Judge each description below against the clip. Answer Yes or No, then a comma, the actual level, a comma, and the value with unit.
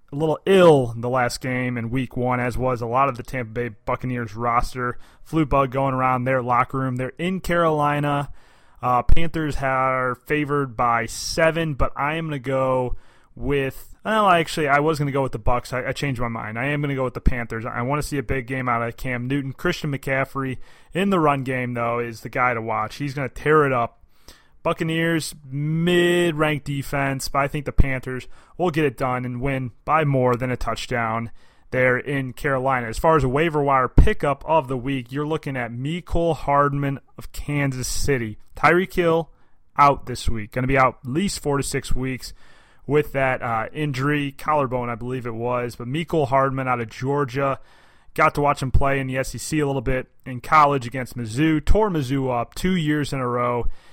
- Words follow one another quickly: Yes, fast, 210 wpm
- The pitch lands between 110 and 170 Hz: Yes, low, 135 Hz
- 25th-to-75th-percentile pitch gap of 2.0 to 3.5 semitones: Yes, average, 2.9 semitones